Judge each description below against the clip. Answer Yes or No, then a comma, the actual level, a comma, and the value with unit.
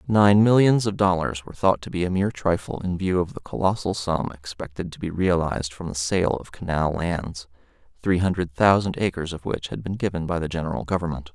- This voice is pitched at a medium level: No, very low, 90 Hz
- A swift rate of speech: Yes, fast, 210 wpm